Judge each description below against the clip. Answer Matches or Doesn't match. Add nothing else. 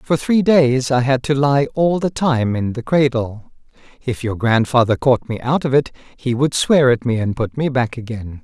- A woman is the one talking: Doesn't match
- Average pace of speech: Doesn't match